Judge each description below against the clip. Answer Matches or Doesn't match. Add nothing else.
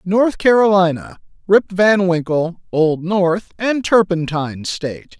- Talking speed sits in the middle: Doesn't match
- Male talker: Matches